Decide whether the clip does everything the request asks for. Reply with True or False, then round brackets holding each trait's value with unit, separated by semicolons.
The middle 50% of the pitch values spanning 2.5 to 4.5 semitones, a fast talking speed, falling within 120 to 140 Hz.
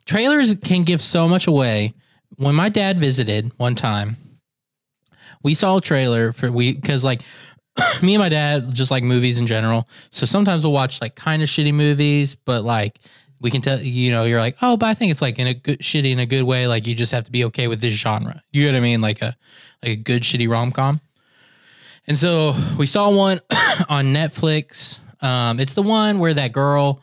True (4.0 semitones; 215 wpm; 135 Hz)